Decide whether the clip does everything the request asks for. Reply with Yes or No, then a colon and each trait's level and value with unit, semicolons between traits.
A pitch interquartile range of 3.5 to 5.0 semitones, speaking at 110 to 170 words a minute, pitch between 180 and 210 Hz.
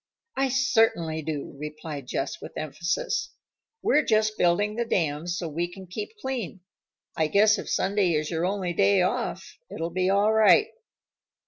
Yes: average, 4.7 semitones; average, 155 wpm; medium, 185 Hz